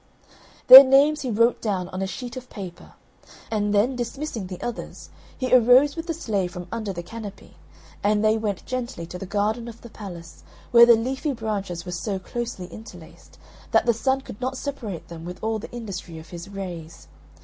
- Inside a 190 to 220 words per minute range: Yes, average, 195 wpm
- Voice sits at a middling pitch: No, high, 215 Hz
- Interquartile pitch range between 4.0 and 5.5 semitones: Yes, average, 4.7 semitones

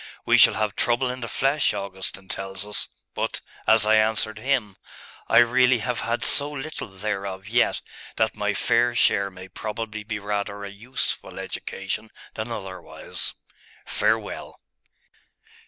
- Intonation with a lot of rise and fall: No, average, 3.1 semitones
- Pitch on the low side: Yes, low, 110 Hz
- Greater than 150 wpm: No, average, 140 wpm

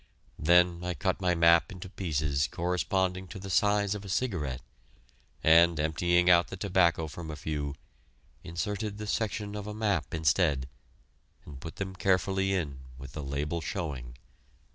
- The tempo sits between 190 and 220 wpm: No, average, 150 wpm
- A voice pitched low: Yes, very low, 85 Hz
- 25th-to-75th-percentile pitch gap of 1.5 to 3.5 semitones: No, average, 3.9 semitones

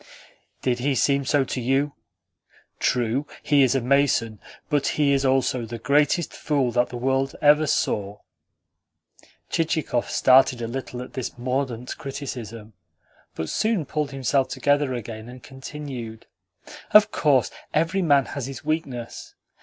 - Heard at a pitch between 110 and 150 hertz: Yes, low, 135 Hz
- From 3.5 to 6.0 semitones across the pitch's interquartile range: No, average, 2.8 semitones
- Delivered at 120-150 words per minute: Yes, average, 140 wpm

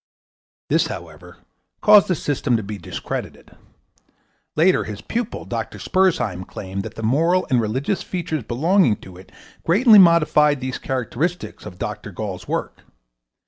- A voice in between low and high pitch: Yes, medium, 145 Hz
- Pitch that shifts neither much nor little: No, wide, 8.3 semitones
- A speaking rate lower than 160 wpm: Yes, average, 140 wpm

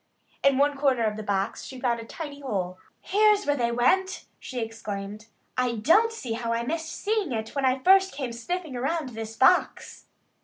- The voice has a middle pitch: No, very high, 255 Hz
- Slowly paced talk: No, average, 190 wpm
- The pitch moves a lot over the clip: Yes, wide, 6.1 semitones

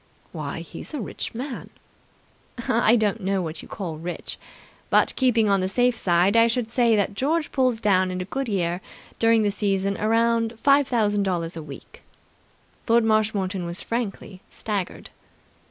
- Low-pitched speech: No, high, 210 Hz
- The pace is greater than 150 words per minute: Yes, average, 165 wpm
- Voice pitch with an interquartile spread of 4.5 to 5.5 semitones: No, average, 3.7 semitones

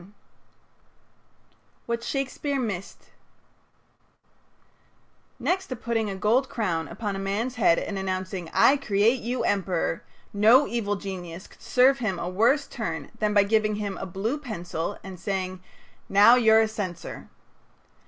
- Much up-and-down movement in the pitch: No, average, 3.9 semitones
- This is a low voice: No, high, 210 Hz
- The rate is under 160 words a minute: Yes, average, 140 wpm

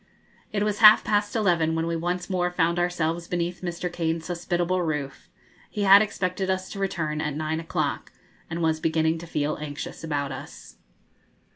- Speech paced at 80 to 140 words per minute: No, average, 170 wpm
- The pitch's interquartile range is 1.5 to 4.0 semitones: Yes, narrow, 2.4 semitones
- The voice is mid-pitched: Yes, medium, 170 Hz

